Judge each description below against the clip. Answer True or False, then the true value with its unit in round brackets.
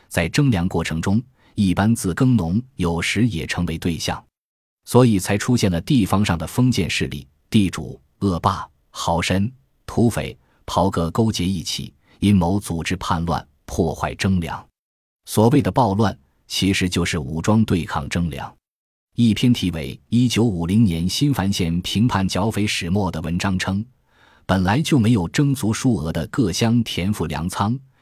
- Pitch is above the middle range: False (95 Hz)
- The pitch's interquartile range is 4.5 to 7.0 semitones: True (5.2 semitones)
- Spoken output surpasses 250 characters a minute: False (235 characters per minute)